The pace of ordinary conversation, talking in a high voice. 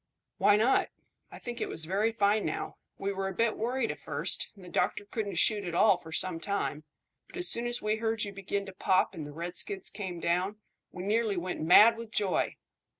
No: fast, 215 wpm; high, 200 Hz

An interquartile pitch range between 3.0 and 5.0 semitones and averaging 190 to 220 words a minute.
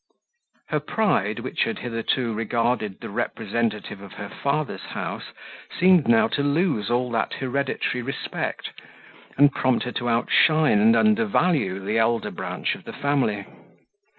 No: average, 4.4 semitones; average, 140 wpm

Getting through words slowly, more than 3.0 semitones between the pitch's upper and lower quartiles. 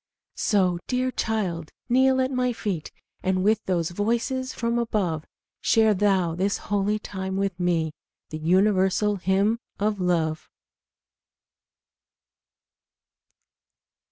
Yes: slow, 110 wpm; average, 3.8 semitones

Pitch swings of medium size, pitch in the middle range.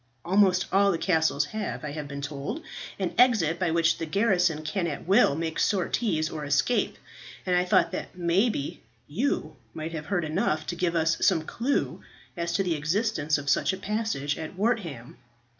Yes: average, 4.2 semitones; medium, 170 Hz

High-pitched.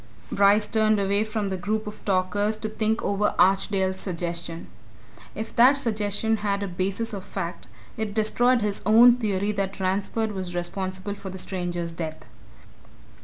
Yes: high, 200 Hz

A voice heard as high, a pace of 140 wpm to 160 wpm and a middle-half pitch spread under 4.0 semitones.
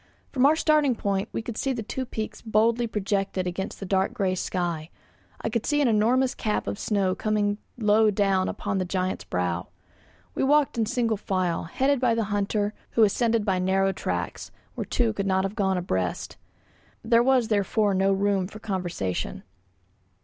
No: high, 205 Hz; average, 180 wpm; average, 3.3 semitones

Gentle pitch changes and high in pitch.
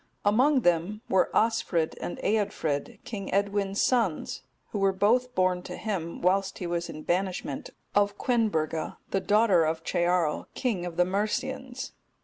No: average, 3.7 semitones; high, 195 Hz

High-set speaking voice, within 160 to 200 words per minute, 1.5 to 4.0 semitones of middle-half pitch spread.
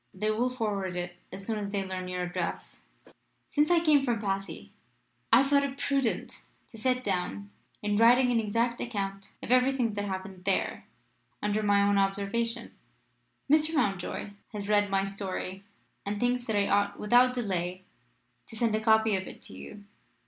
Yes: high, 210 Hz; average, 180 wpm; average, 3.7 semitones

